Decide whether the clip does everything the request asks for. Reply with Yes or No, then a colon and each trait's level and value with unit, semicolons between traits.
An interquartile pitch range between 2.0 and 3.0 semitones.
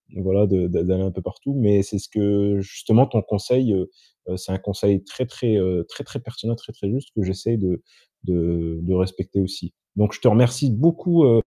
No: average, 3.5 semitones